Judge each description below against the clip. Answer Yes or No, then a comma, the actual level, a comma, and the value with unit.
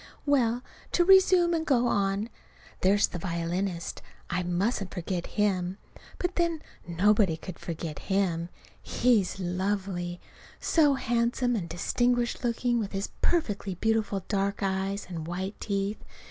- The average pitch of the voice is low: No, high, 200 Hz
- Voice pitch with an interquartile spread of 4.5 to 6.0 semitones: Yes, average, 4.8 semitones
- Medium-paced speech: No, slow, 130 wpm